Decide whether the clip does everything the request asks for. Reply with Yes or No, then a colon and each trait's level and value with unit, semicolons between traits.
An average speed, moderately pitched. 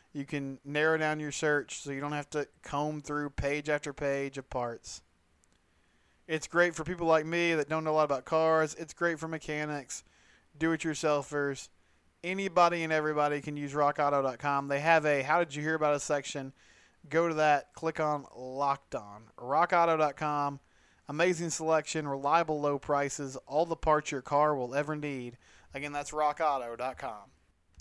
Yes: average, 165 wpm; medium, 145 Hz